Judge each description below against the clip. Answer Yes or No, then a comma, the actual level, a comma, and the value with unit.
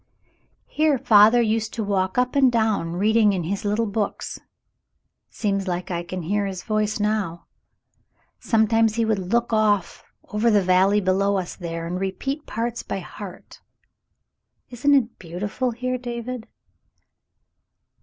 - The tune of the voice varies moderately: Yes, average, 3.5 semitones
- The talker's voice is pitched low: No, high, 210 Hz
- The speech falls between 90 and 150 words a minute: Yes, average, 145 wpm